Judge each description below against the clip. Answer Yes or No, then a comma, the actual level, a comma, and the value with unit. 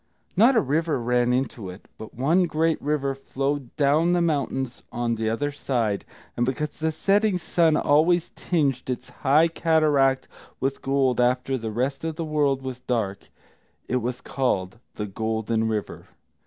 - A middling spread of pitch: Yes, average, 4.2 semitones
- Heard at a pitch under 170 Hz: Yes, low, 135 Hz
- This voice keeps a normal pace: Yes, average, 160 wpm